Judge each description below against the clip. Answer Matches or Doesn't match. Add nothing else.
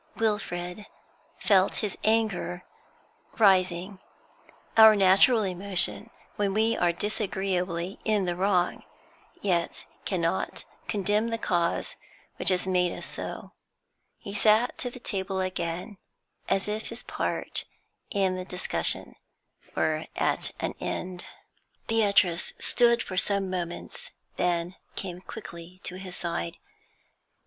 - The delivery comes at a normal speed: Doesn't match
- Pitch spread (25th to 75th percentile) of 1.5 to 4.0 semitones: Matches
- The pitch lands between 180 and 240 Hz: Matches